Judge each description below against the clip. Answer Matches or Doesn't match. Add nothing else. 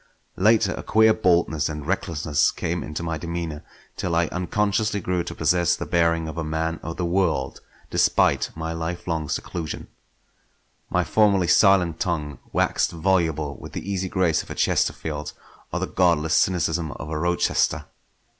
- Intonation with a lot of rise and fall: Doesn't match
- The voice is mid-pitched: Doesn't match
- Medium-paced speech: Matches